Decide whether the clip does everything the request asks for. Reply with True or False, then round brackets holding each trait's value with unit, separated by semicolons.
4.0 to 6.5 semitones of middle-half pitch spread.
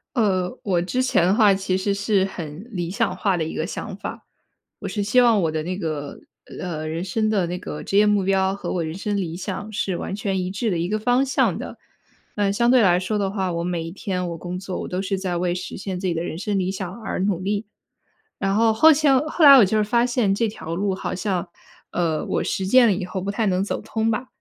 False (2.9 semitones)